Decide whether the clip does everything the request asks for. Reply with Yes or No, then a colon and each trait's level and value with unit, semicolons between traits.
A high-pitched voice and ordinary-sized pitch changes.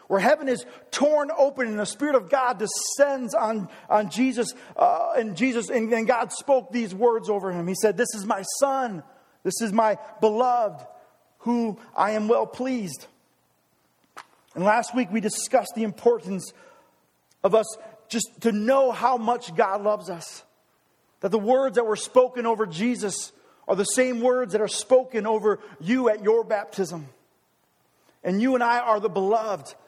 Yes: high, 225 Hz; average, 3.2 semitones